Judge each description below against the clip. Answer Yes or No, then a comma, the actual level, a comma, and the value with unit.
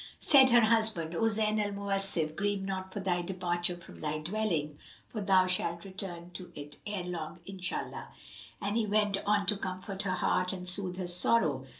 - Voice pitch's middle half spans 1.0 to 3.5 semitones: Yes, narrow, 2.6 semitones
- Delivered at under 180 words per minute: No, average, 185 wpm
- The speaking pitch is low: No, high, 190 Hz